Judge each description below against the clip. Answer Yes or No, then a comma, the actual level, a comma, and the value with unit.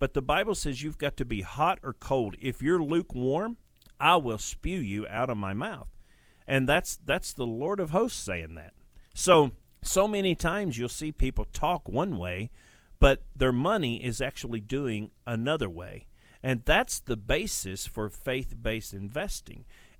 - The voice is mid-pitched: No, low, 120 Hz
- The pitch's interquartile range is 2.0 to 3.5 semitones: No, wide, 5.6 semitones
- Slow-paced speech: No, average, 170 wpm